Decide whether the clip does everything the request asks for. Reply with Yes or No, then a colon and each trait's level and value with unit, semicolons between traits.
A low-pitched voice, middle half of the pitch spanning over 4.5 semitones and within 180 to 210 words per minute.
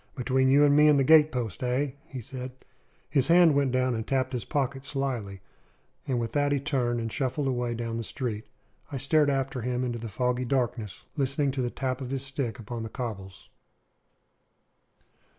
No: low, 130 Hz; narrow, 2.4 semitones; average, 185 wpm